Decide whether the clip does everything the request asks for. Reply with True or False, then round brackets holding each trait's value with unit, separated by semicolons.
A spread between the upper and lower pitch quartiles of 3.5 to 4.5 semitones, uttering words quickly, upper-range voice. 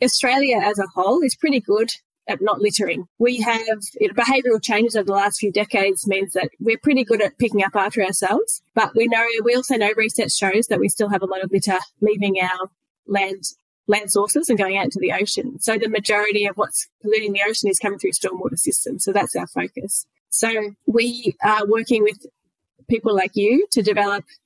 False (2.6 semitones; 210 wpm; 210 Hz)